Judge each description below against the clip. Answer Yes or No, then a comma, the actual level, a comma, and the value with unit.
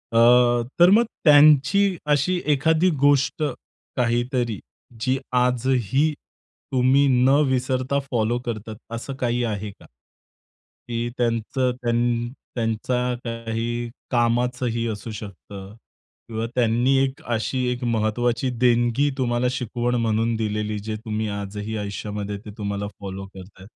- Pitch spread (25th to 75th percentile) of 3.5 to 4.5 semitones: No, average, 2.8 semitones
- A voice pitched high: No, low, 120 Hz